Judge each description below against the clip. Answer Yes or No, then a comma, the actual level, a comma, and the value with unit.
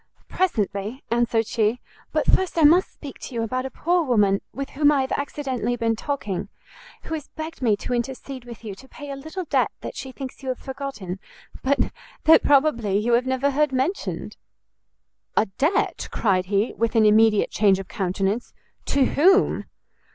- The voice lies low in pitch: No, very high, 255 Hz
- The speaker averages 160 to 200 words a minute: Yes, average, 180 wpm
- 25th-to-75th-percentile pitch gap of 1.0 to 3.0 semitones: No, average, 4.7 semitones